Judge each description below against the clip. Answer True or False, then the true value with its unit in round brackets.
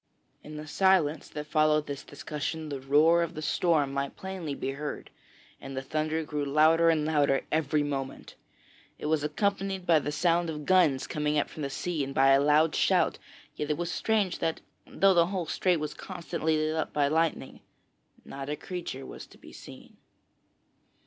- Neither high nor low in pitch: True (155 Hz)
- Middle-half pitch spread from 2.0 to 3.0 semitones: True (2.5 semitones)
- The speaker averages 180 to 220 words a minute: True (185 wpm)